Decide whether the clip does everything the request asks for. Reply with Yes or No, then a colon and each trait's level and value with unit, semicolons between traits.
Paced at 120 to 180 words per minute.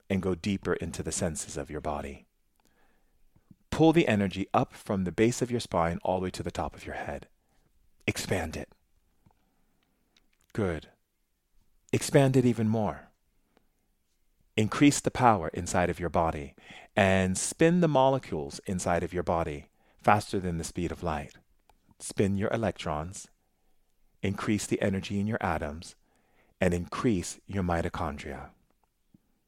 Yes: average, 140 wpm